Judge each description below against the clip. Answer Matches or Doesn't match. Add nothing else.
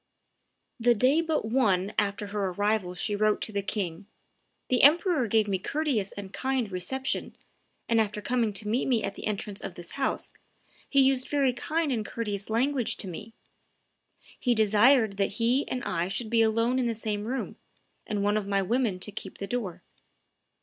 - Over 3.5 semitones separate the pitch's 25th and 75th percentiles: Matches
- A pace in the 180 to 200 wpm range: Matches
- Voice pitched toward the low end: Doesn't match